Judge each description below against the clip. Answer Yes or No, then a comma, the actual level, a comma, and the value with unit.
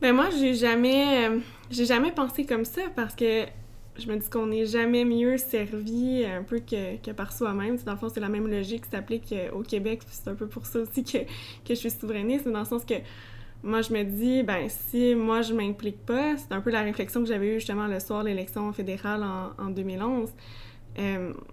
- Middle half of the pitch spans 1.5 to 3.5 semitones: Yes, average, 3.0 semitones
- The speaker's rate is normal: No, fast, 230 wpm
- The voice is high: Yes, high, 225 Hz